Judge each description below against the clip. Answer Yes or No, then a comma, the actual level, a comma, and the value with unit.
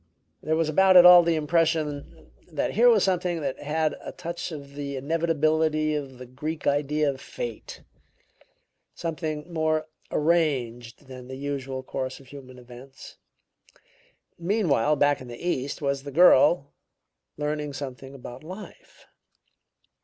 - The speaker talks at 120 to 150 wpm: Yes, average, 140 wpm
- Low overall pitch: No, medium, 150 Hz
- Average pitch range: Yes, average, 3.4 semitones